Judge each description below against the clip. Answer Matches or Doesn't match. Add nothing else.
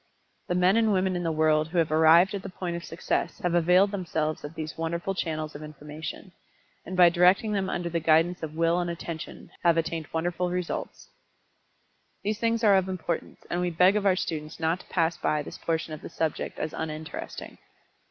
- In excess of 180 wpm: Matches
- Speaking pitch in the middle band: Matches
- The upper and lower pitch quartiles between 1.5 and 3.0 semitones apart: Matches